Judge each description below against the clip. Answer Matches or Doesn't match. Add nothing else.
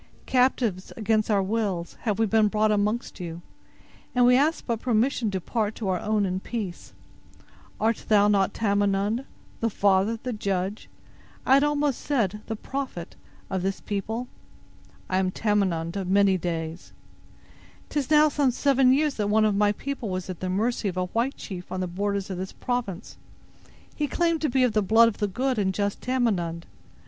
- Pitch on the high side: Matches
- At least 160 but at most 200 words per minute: Matches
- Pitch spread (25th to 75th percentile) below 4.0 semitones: Doesn't match